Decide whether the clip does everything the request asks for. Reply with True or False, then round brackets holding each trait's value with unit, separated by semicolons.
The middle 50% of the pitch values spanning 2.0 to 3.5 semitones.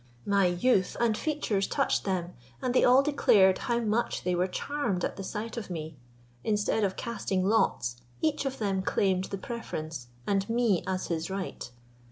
False (4.1 semitones)